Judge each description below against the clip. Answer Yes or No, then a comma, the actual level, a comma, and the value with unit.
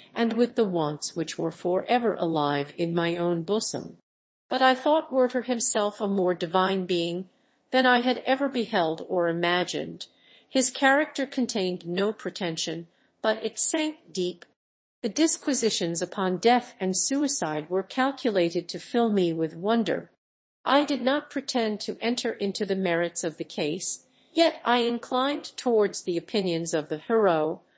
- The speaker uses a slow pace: No, average, 155 wpm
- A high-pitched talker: Yes, high, 205 Hz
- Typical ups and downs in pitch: No, wide, 6.5 semitones